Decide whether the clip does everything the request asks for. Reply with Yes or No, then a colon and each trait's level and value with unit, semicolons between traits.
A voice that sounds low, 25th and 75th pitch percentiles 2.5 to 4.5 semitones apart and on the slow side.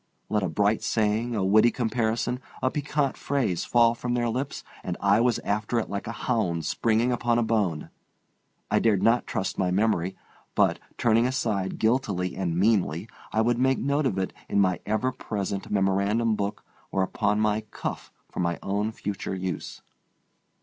No: low, 110 Hz; average, 3.5 semitones; average, 175 wpm